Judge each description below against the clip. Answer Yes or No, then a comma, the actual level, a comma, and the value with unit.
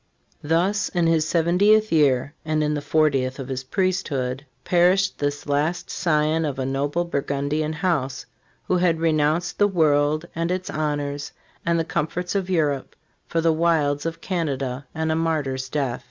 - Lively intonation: No, average, 3.0 semitones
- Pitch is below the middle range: No, medium, 155 Hz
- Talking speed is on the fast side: No, average, 165 wpm